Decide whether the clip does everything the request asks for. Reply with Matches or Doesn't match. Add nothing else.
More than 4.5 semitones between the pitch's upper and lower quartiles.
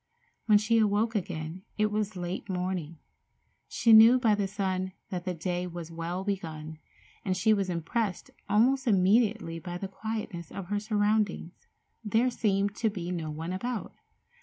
Doesn't match